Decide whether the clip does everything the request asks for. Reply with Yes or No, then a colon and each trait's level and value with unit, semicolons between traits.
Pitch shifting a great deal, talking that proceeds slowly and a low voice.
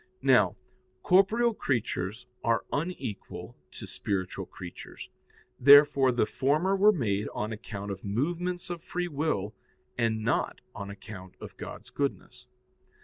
Yes: wide, 7.8 semitones; slow, 125 wpm; low, 125 Hz